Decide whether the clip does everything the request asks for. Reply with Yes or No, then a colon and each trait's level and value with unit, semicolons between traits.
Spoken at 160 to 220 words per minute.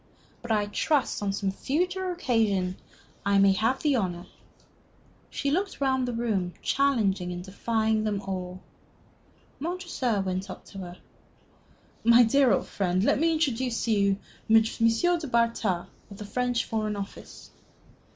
No: average, 150 wpm